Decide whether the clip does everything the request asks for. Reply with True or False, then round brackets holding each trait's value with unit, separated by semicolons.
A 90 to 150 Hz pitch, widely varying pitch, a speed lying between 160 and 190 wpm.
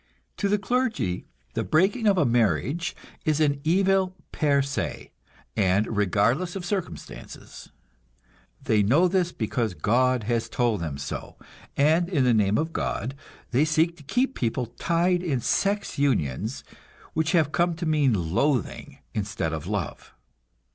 False (140 Hz; 7.9 semitones; 145 wpm)